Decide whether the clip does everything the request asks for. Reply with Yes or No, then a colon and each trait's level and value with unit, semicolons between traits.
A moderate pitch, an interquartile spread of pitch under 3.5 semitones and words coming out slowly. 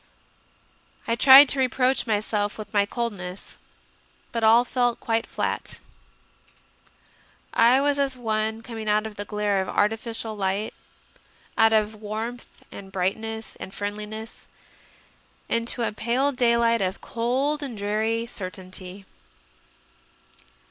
No: high, 220 Hz; narrow, 2.4 semitones; slow, 120 wpm